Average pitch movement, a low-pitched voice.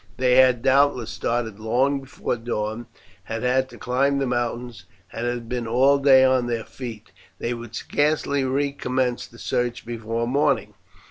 No: narrow, 2.2 semitones; low, 125 Hz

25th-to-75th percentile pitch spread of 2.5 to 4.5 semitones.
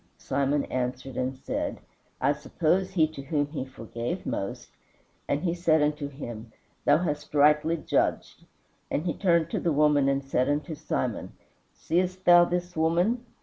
Yes: average, 3.8 semitones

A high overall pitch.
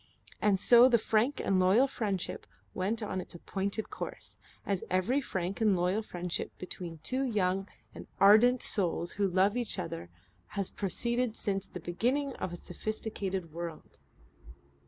Yes: high, 195 Hz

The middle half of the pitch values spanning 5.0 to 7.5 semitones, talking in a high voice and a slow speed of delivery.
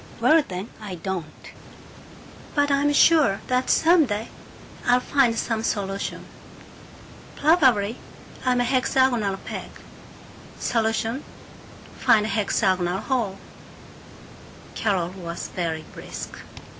Yes: average, 5.3 semitones; high, 225 Hz; slow, 100 wpm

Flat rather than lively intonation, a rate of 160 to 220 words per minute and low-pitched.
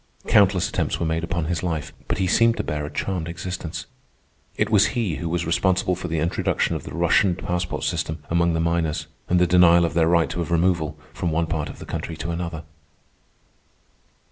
Yes: narrow, 1.6 semitones; average, 200 wpm; very low, 85 Hz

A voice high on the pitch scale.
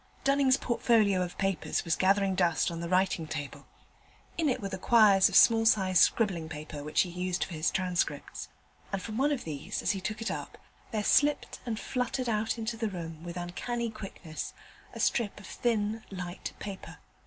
Yes: high, 195 Hz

